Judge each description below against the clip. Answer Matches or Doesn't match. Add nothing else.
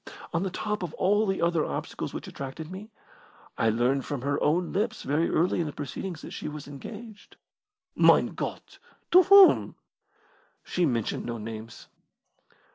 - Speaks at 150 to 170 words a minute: Matches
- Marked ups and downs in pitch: Matches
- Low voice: Doesn't match